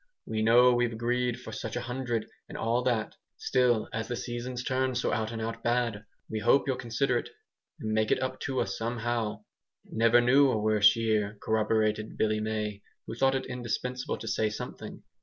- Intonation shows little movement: Yes, narrow, 2.2 semitones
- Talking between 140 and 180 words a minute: No, average, 195 wpm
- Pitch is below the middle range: Yes, low, 115 Hz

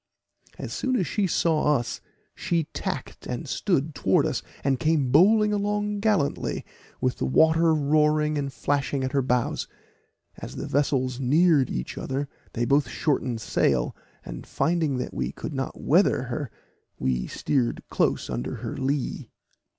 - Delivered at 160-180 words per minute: No, average, 150 wpm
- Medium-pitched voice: Yes, medium, 145 Hz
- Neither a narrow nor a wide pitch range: Yes, average, 4.1 semitones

